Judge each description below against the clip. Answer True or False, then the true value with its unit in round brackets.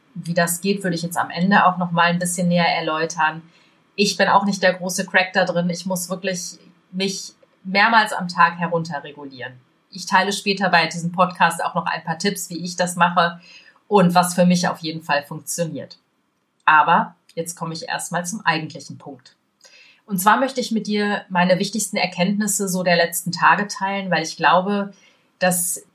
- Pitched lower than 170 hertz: False (180 Hz)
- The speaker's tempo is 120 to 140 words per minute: False (185 wpm)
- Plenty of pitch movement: False (2.5 semitones)